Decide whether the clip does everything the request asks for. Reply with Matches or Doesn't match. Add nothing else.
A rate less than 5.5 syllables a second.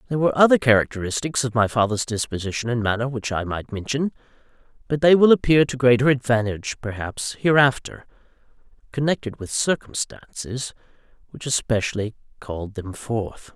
Doesn't match